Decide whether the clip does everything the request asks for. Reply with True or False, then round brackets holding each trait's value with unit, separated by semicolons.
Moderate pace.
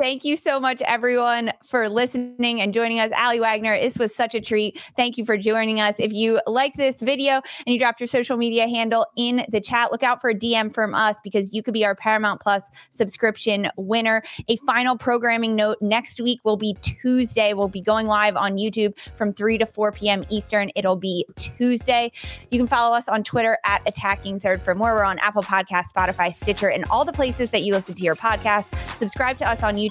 False (220 wpm)